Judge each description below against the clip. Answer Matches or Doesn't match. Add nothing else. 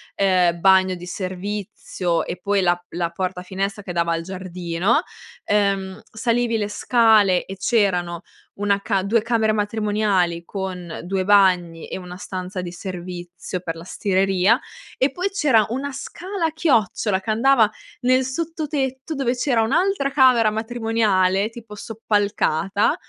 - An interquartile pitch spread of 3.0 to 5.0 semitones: Matches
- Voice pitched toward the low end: Doesn't match